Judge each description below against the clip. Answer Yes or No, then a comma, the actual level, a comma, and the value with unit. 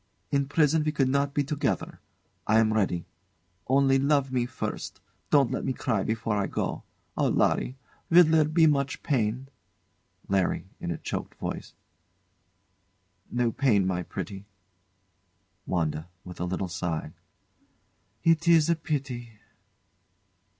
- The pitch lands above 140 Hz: No, low, 130 Hz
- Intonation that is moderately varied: No, wide, 6.3 semitones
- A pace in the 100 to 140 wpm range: Yes, slow, 135 wpm